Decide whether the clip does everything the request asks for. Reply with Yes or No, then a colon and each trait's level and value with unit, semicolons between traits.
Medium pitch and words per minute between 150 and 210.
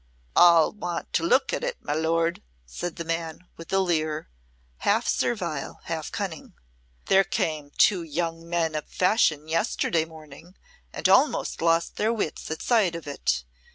Yes: medium, 165 Hz; average, 155 wpm